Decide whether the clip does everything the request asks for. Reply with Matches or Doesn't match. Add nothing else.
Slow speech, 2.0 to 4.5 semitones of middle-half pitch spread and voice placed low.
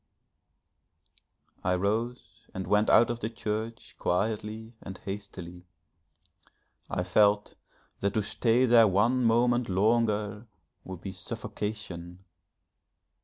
Matches